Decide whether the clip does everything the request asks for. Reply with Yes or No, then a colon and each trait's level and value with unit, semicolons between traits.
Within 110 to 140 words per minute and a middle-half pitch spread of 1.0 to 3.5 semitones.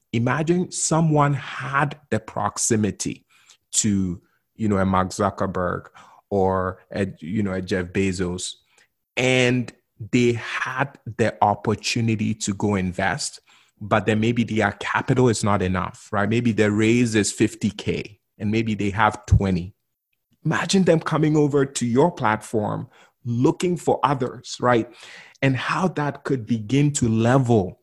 No: slow, 135 wpm; average, 4.7 semitones